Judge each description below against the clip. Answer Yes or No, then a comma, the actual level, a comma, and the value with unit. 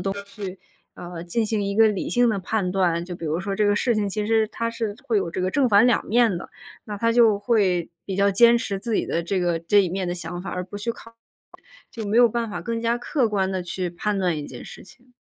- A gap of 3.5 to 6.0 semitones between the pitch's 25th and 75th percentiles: Yes, average, 3.9 semitones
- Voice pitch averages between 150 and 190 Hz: No, high, 205 Hz